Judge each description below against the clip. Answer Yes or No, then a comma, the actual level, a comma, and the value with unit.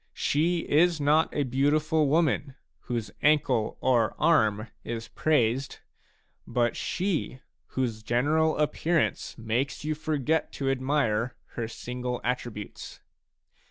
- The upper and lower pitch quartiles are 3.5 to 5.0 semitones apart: Yes, average, 4.4 semitones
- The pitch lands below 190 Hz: Yes, low, 135 Hz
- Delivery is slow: Yes, slow, 110 wpm